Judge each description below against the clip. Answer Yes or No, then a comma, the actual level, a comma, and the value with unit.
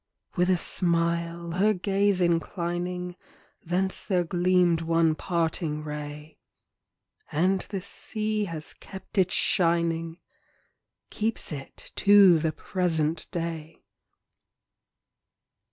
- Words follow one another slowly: Yes, slow, 100 wpm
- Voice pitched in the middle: Yes, medium, 170 Hz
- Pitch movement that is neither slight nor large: No, narrow, 2.2 semitones